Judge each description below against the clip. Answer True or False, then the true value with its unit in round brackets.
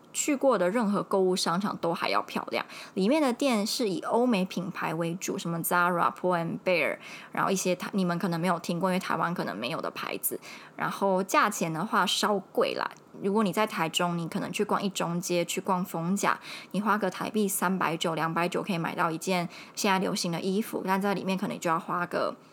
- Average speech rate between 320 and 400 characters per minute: True (335 characters per minute)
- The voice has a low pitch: False (190 Hz)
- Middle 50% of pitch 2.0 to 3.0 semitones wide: True (2.6 semitones)